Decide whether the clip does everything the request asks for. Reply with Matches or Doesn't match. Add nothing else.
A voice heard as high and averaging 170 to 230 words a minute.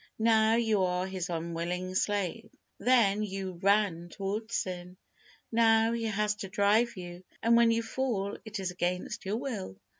Doesn't match